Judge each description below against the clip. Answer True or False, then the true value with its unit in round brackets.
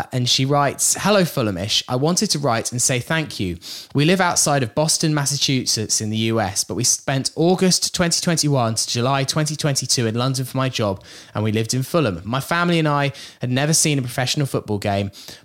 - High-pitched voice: False (135 Hz)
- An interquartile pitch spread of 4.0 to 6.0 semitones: True (5.0 semitones)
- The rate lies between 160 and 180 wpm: False (200 wpm)